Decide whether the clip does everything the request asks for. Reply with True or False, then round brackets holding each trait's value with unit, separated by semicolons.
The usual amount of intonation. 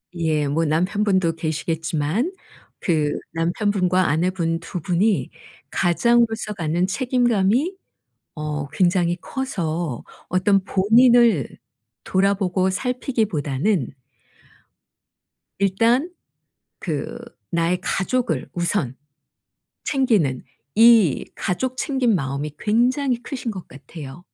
False (5.9 semitones)